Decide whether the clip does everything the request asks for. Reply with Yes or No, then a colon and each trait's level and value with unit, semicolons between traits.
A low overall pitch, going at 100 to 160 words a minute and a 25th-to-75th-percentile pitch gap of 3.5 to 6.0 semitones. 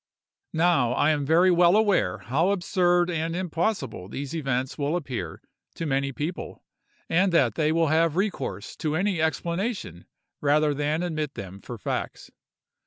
No: medium, 160 Hz; average, 150 wpm; average, 4.1 semitones